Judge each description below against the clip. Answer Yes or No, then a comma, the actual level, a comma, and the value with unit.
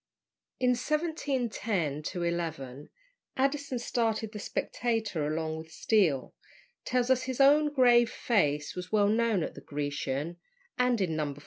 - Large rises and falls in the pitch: Yes, wide, 7.9 semitones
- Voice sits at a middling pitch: No, high, 215 Hz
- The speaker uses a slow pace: Yes, slow, 130 wpm